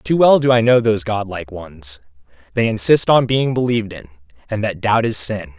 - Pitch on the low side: Yes, low, 105 Hz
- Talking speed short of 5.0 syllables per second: No, 5.5 syllables/s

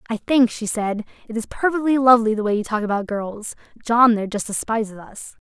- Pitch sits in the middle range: No, high, 225 Hz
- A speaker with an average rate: No, fast, 210 wpm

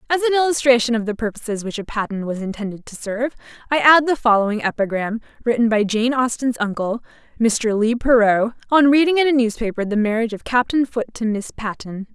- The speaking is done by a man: No, female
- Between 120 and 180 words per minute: No, average, 195 wpm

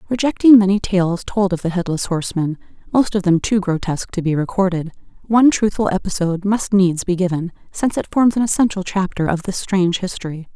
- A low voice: No, high, 190 Hz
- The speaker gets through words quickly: No, average, 175 wpm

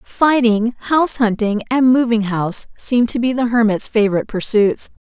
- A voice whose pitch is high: Yes, high, 230 Hz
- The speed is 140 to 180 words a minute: Yes, average, 155 wpm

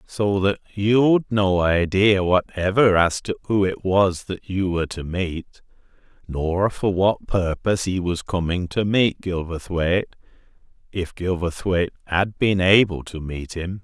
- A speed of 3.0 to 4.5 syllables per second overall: Yes, 4.1 syllables/s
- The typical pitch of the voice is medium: No, very low, 95 Hz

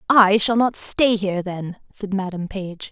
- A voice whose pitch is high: Yes, high, 200 Hz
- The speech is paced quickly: No, average, 185 wpm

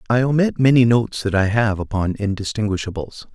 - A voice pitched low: Yes, low, 110 Hz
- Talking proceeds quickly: No, average, 160 wpm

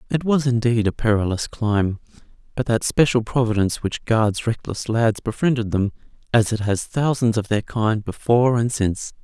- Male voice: Yes, male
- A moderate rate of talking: Yes, average, 170 wpm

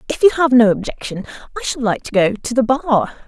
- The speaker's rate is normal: No, fast, 240 wpm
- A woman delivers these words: Yes, female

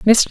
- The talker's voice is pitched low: No, high, 215 Hz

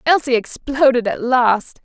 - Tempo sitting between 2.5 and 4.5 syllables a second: Yes, 4.1 syllables/s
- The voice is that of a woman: Yes, female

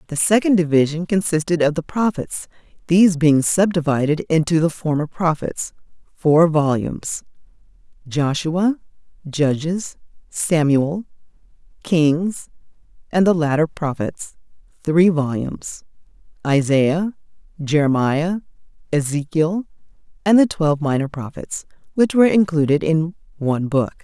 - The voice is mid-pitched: Yes, medium, 160 Hz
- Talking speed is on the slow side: Yes, slow, 90 wpm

